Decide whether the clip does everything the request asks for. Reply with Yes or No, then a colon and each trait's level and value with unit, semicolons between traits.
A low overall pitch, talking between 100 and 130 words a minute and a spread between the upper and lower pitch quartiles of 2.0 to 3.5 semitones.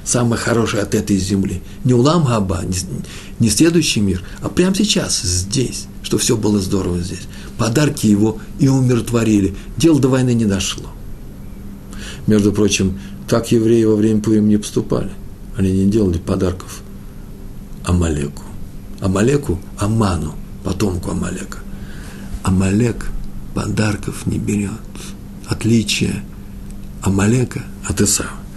Yes: low, 100 Hz; average, 115 wpm; average, 3.0 semitones